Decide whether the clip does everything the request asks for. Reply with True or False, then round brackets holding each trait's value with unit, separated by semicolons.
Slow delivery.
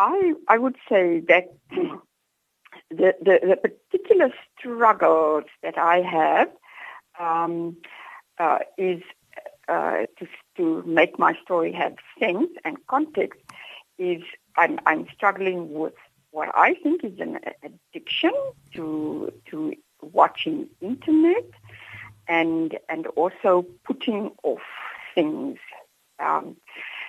True (105 wpm)